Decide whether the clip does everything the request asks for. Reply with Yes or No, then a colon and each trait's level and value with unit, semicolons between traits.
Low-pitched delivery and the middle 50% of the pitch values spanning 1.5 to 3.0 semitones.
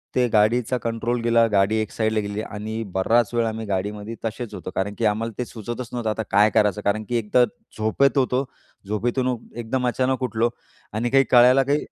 Yes: low, 115 Hz; narrow, 2.4 semitones